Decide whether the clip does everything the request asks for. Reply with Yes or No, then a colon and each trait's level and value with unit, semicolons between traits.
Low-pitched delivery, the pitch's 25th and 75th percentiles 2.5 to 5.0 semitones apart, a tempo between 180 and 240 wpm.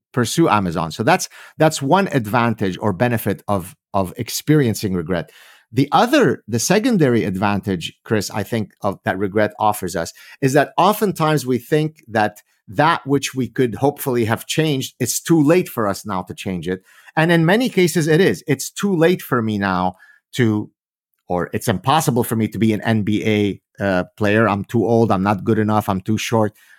No: low, 115 Hz; wide, 5.4 semitones; average, 185 wpm